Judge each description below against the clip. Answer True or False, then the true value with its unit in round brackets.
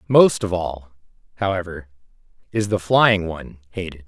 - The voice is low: True (90 Hz)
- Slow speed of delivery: True (130 wpm)